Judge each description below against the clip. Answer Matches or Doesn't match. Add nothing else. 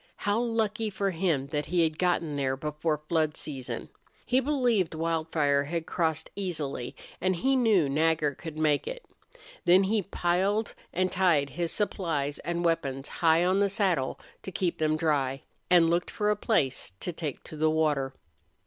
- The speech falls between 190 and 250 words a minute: Doesn't match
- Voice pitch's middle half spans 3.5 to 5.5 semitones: Matches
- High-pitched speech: Doesn't match